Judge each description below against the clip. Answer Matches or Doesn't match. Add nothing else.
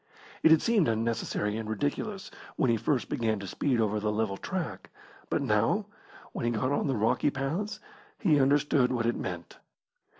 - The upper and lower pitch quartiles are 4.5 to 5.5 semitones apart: Matches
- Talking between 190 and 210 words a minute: Doesn't match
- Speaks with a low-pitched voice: Matches